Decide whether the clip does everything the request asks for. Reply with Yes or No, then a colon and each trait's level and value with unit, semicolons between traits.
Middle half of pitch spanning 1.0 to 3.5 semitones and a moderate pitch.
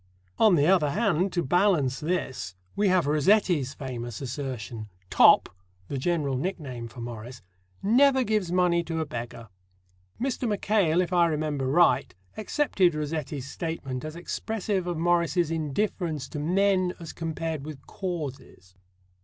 No: average, 5.2 semitones; medium, 160 Hz